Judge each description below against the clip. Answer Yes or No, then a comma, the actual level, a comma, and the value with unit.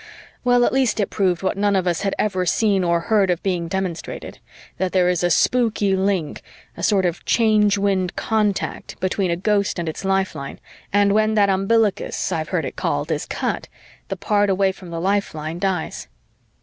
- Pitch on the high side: Yes, high, 195 Hz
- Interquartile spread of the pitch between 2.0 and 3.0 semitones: Yes, narrow, 2.4 semitones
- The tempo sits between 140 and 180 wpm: No, average, 190 wpm